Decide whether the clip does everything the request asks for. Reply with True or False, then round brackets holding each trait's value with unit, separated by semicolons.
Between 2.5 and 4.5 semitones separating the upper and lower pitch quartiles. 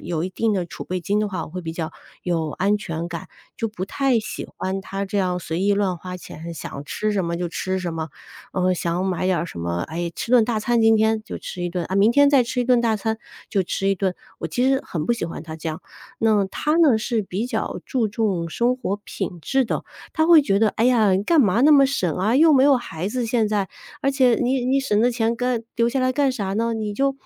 False (5.1 semitones)